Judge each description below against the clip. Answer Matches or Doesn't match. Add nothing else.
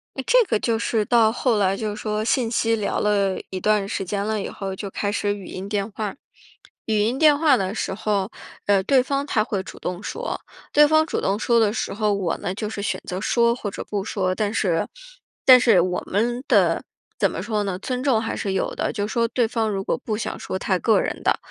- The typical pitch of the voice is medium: Doesn't match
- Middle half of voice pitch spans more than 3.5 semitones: Doesn't match